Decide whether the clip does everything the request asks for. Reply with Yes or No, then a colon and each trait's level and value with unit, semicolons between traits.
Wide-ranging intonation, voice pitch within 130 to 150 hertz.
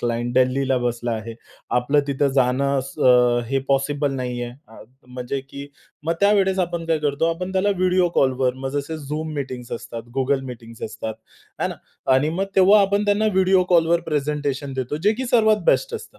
Yes: wide, 6.1 semitones; medium, 140 Hz